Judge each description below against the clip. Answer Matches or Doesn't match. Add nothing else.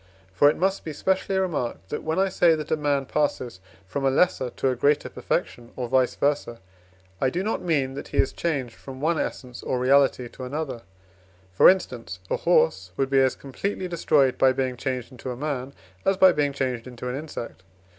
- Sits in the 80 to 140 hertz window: Matches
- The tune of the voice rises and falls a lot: Doesn't match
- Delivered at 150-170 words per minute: Doesn't match